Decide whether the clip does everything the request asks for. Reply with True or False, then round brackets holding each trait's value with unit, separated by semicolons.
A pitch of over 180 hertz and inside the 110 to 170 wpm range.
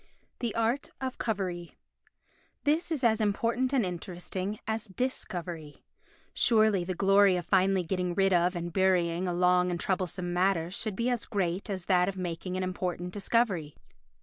True (190 Hz; 165 wpm)